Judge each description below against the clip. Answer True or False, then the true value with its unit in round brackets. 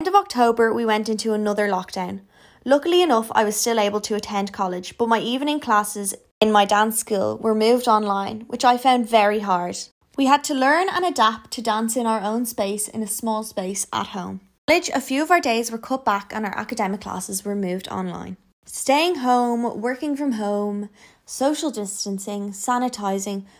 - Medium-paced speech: True (190 wpm)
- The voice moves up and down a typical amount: True (3.4 semitones)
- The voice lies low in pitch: False (220 Hz)